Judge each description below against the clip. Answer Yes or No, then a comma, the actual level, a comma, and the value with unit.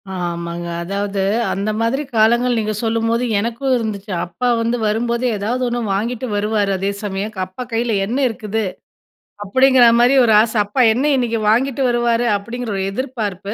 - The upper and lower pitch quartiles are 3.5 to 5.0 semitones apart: No, average, 3.1 semitones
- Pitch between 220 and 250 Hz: Yes, high, 225 Hz